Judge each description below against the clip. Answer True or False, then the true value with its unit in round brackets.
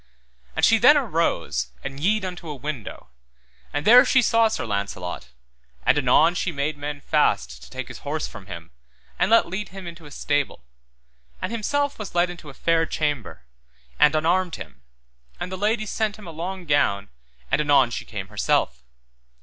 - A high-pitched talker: False (150 Hz)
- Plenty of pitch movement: True (7.2 semitones)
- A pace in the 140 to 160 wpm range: False (180 wpm)